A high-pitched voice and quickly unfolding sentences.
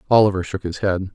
No: very low, 95 Hz; fast, 210 wpm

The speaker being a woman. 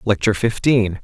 No: male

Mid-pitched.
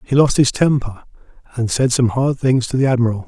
No: low, 125 Hz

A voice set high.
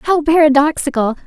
Yes: very high, 295 Hz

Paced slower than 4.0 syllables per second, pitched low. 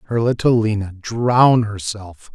Yes: 3.8 syllables/s; low, 110 Hz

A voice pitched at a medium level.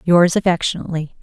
Yes: medium, 175 Hz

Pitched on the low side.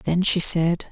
No: medium, 175 Hz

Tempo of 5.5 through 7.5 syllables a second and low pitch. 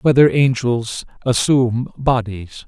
No: 3.8 syllables/s; low, 125 Hz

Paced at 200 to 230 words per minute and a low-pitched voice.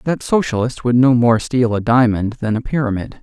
Yes: fast, 205 wpm; low, 120 Hz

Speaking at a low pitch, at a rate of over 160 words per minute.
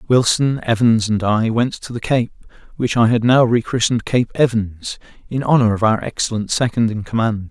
Yes: low, 115 Hz; average, 185 wpm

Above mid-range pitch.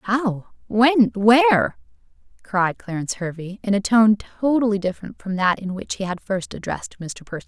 Yes: high, 205 Hz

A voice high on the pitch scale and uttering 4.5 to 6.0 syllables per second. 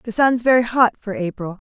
Yes: high, 220 Hz; 5.5 syllables/s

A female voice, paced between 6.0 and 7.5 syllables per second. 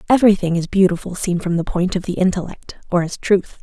Yes: female; 6.1 syllables/s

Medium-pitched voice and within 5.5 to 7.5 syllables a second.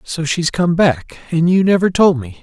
No: medium, 170 Hz; 4.5 syllables/s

